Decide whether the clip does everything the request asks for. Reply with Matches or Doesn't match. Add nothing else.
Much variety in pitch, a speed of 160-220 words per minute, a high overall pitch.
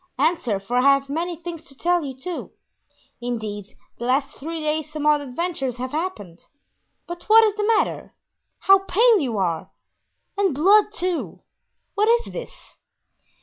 Doesn't match